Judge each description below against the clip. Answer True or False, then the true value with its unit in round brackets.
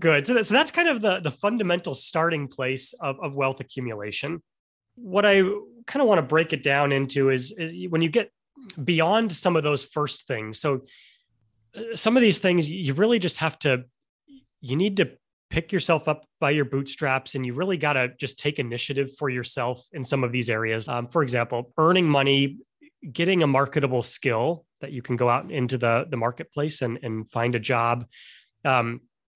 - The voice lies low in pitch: False (145 Hz)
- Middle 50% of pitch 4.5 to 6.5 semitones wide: True (5.3 semitones)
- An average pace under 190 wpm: False (195 wpm)